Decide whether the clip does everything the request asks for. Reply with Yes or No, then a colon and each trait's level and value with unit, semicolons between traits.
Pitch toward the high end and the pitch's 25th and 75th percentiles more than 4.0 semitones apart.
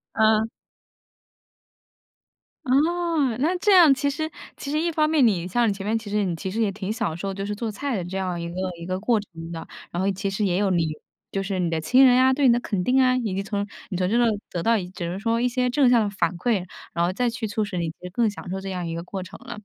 Yes: high, 210 Hz; average, 5.2 semitones